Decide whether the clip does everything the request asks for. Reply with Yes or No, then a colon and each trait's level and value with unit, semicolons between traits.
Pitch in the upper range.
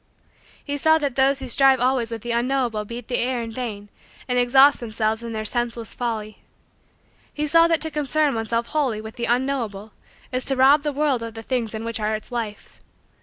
Yes: high, 245 Hz